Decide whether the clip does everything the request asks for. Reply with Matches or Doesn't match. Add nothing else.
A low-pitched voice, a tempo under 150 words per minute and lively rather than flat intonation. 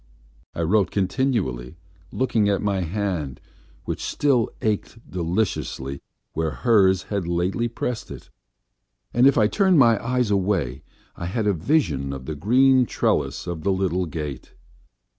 Matches